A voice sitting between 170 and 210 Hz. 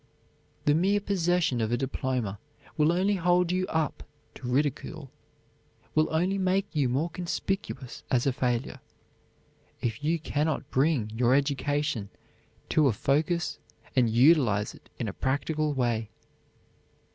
No: medium, 145 Hz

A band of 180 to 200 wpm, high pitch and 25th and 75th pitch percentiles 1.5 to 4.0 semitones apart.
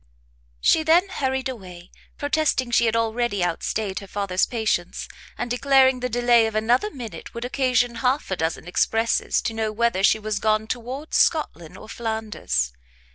No: average, 160 wpm; high, 230 Hz; average, 3.2 semitones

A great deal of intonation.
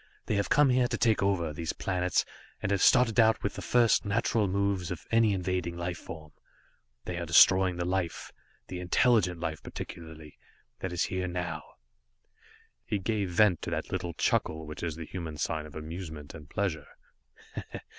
No: average, 3.5 semitones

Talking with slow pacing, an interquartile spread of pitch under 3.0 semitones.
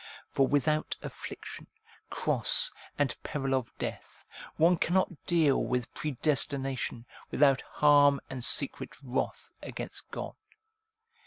Yes: slow, 105 wpm; narrow, 2.4 semitones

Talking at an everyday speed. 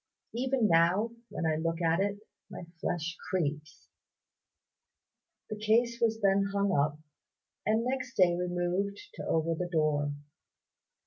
No: slow, 130 wpm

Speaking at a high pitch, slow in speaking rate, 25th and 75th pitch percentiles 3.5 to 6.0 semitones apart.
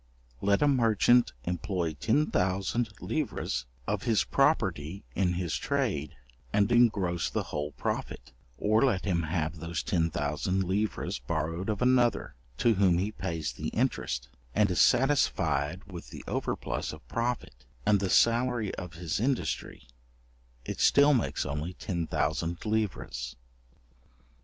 No: very low, 95 Hz; slow, 130 wpm; average, 5.3 semitones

